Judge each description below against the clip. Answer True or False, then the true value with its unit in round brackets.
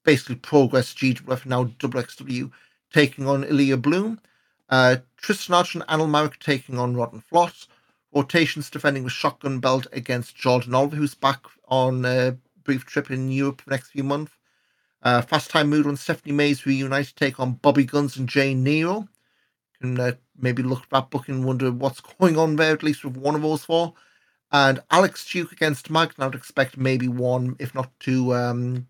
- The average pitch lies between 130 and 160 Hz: True (135 Hz)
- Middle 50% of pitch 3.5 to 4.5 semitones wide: False (2.7 semitones)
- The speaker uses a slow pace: False (190 wpm)